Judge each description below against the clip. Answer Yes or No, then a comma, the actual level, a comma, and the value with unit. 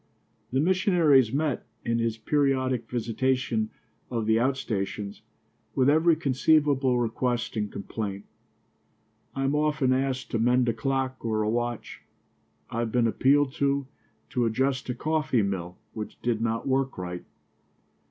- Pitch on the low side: Yes, low, 125 Hz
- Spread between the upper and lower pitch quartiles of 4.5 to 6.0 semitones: No, average, 3.3 semitones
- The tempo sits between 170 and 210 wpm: No, average, 140 wpm